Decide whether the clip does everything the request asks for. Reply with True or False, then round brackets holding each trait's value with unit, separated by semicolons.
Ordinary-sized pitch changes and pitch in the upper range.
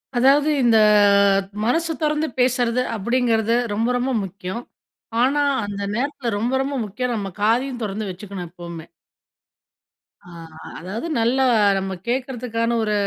True (3.7 semitones; 235 Hz)